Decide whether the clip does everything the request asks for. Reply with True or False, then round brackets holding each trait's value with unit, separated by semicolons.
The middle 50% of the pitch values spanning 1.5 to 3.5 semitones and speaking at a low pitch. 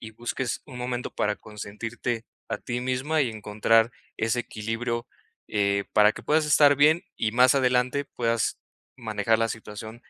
True (2.5 semitones; 115 Hz)